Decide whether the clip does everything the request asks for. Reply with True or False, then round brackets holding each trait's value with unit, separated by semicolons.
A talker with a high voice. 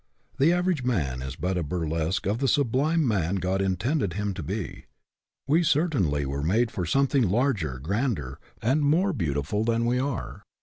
False (105 Hz)